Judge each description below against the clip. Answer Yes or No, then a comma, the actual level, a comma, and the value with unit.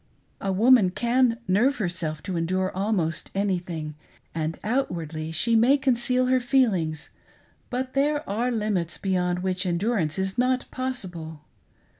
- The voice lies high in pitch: Yes, high, 195 Hz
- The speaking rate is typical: No, slow, 130 wpm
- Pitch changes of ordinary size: No, wide, 6.3 semitones